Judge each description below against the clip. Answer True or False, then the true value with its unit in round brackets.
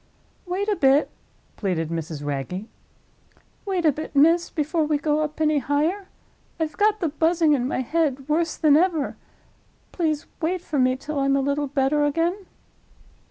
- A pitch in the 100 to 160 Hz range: False (300 Hz)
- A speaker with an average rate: True (160 wpm)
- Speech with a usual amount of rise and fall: True (3.3 semitones)